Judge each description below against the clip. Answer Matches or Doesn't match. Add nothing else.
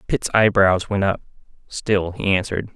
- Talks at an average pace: Matches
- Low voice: Matches